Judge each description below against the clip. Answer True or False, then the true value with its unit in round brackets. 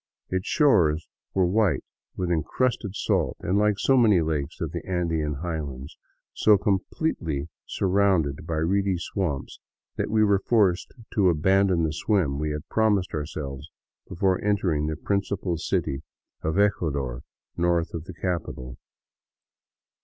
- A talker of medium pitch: False (85 Hz)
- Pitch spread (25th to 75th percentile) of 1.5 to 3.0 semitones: False (4.3 semitones)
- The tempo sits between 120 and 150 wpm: True (140 wpm)